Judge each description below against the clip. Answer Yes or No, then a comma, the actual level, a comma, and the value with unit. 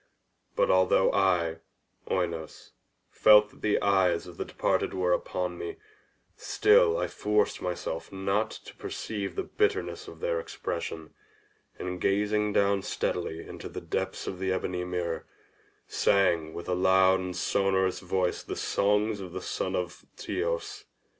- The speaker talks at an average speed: Yes, average, 145 wpm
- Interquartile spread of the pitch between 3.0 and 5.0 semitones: No, narrow, 2.6 semitones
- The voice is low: Yes, very low, 95 Hz